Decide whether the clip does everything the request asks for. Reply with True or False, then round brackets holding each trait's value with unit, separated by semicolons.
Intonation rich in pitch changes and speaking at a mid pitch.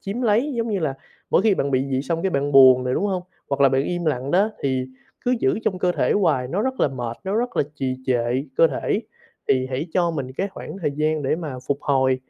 True (6.4 semitones; 145 Hz)